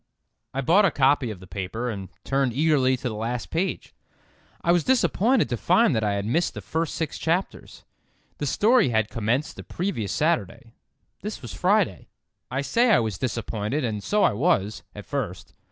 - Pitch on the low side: Yes, low, 130 Hz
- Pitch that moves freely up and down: Yes, wide, 7.3 semitones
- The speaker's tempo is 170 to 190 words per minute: Yes, average, 185 wpm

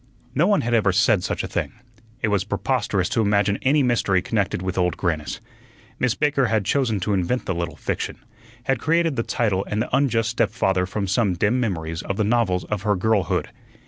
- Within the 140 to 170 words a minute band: No, average, 200 wpm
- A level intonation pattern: No, average, 4.3 semitones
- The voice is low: Yes, low, 105 Hz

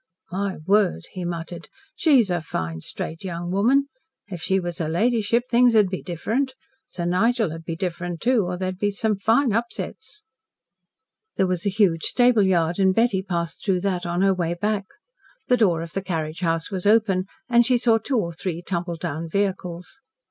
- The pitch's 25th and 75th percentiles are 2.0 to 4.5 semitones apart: Yes, average, 4.2 semitones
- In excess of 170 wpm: Yes, average, 185 wpm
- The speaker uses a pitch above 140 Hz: Yes, high, 190 Hz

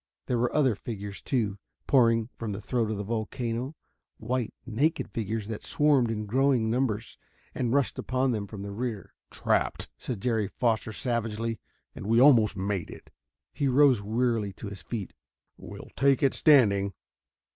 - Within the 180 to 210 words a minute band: No, average, 165 wpm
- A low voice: Yes, low, 115 Hz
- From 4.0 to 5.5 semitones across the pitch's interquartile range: No, average, 3.4 semitones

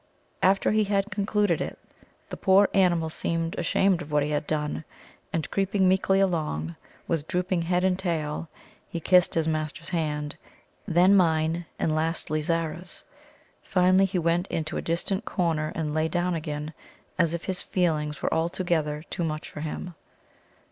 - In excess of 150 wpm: Yes, average, 160 wpm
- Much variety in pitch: No, average, 3.0 semitones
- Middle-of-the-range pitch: Yes, medium, 170 Hz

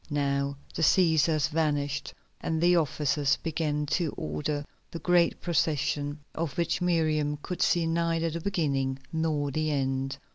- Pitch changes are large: No, narrow, 2.5 semitones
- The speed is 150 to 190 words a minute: No, average, 140 wpm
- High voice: No, medium, 155 Hz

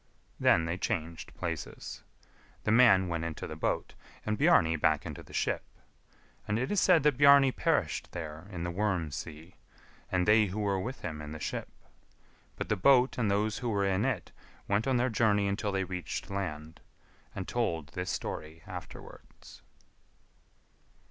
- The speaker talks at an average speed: Yes, average, 170 wpm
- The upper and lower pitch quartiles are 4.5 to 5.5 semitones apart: Yes, average, 5.1 semitones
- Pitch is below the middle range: Yes, very low, 95 Hz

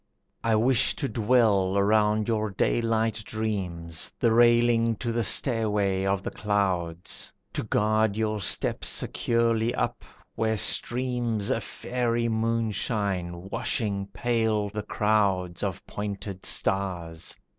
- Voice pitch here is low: Yes, low, 110 Hz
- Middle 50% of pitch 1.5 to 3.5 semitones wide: Yes, average, 2.7 semitones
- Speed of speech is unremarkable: No, slow, 115 wpm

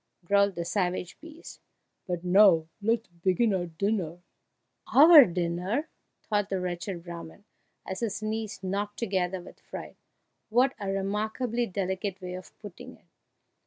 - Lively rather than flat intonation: No, average, 3.3 semitones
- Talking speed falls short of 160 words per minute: Yes, average, 140 wpm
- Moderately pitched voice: No, high, 195 Hz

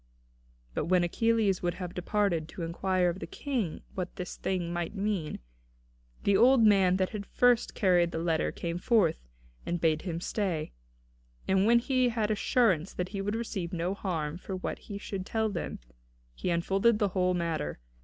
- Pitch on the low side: No, medium, 185 Hz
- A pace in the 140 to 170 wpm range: No, average, 185 wpm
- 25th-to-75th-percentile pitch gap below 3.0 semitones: No, average, 3.5 semitones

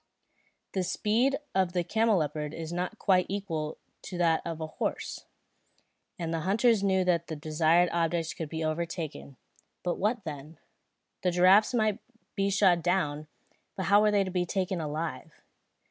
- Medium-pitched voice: Yes, medium, 175 Hz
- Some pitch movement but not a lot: Yes, average, 3.5 semitones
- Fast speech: No, average, 160 wpm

